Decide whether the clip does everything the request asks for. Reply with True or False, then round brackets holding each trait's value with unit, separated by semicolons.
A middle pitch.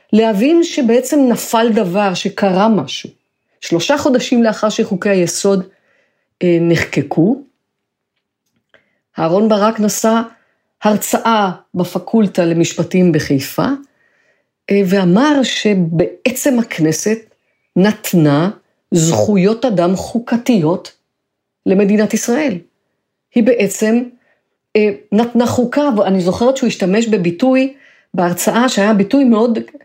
False (215 Hz)